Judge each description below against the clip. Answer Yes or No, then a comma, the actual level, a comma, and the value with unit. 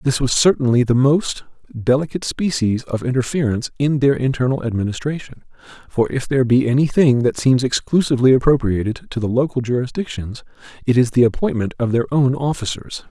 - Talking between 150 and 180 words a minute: Yes, average, 160 wpm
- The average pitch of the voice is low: Yes, low, 130 Hz